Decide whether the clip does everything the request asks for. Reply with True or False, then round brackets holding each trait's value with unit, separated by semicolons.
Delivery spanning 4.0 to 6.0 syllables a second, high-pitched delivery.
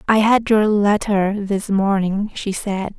False (3.6 syllables/s; 205 Hz)